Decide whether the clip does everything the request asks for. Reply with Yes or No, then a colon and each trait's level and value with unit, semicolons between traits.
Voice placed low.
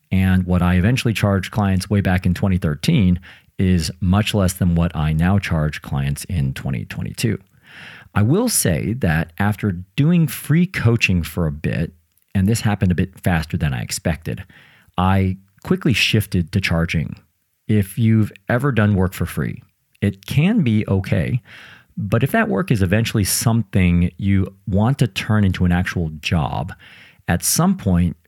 Yes: very low, 95 Hz